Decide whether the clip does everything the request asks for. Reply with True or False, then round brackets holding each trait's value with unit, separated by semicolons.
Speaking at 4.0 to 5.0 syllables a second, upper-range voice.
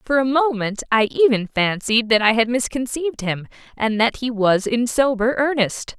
True (4.7 syllables/s; 235 Hz)